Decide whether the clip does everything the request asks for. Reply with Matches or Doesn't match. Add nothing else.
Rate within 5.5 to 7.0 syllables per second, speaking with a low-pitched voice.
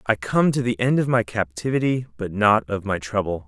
Doesn't match